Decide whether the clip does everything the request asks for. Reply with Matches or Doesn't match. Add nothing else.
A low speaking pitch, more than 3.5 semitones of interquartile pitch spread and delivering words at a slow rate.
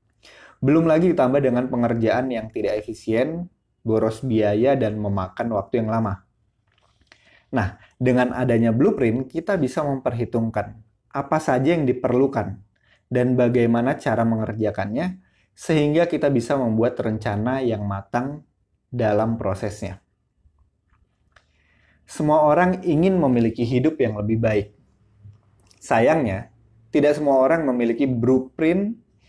Doesn't match